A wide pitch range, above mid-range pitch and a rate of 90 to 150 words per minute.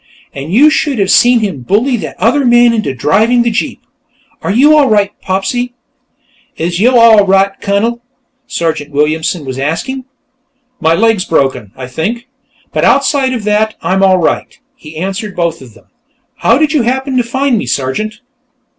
No: wide, 6.6 semitones; high, 210 Hz; average, 170 wpm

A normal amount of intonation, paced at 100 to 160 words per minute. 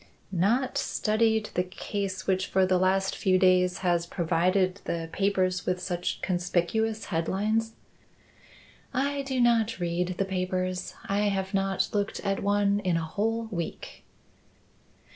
No: narrow, 2.3 semitones; slow, 135 wpm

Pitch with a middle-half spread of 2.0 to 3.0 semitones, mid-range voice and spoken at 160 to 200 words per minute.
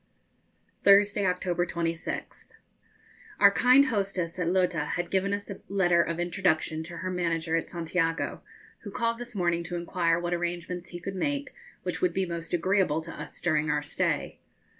Yes: average, 2.7 semitones; medium, 175 Hz; average, 170 wpm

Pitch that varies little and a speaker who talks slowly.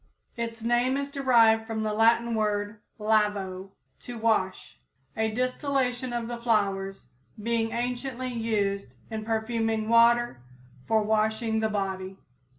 Yes: narrow, 2.1 semitones; slow, 125 wpm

